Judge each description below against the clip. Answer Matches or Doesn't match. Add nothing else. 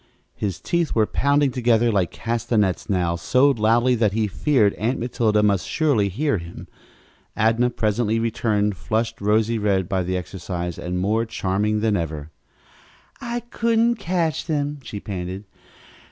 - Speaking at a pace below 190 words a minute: Matches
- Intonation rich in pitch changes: Doesn't match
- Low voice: Matches